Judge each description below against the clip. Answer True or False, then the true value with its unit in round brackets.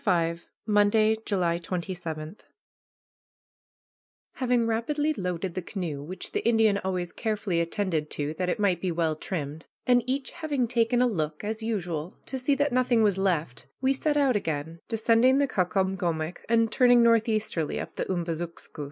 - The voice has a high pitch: True (195 Hz)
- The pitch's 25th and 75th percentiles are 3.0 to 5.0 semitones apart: False (5.6 semitones)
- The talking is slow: False (155 wpm)